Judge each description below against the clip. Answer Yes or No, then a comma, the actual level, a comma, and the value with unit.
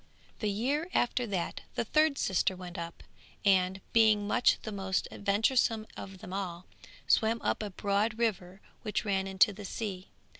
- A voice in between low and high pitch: No, high, 200 Hz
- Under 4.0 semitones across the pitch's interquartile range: Yes, average, 2.8 semitones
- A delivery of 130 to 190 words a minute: Yes, average, 160 wpm